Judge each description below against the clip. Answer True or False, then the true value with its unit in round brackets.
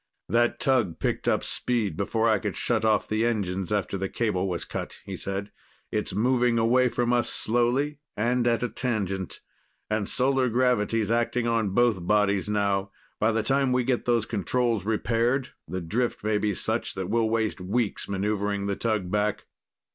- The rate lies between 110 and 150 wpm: False (175 wpm)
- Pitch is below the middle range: True (110 Hz)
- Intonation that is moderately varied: True (3.2 semitones)